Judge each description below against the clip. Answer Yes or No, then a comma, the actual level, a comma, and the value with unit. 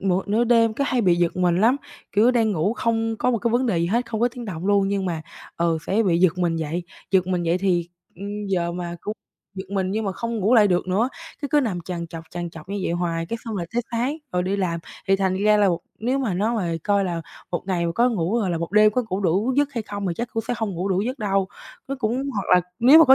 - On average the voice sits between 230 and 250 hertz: No, high, 195 Hz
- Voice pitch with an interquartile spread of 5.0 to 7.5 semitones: No, average, 4.4 semitones